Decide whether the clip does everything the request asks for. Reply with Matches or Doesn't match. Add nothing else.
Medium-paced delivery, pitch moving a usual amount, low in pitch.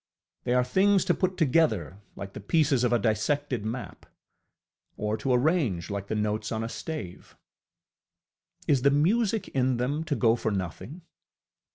Doesn't match